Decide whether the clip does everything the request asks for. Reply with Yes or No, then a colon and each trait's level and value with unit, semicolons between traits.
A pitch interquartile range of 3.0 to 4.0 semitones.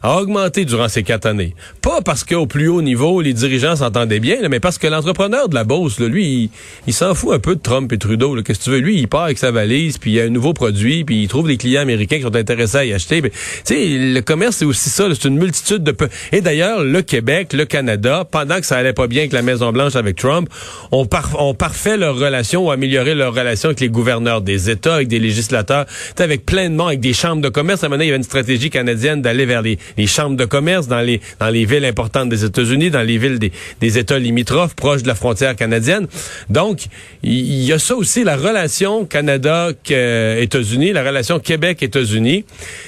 No: average, 4.7 semitones